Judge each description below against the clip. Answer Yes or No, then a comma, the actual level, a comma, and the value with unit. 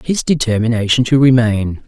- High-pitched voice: No, low, 120 Hz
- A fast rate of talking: No, slow, 130 wpm